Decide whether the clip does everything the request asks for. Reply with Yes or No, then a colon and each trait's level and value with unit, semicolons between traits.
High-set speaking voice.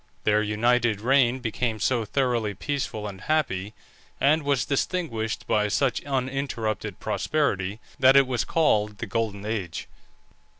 No: low, 115 Hz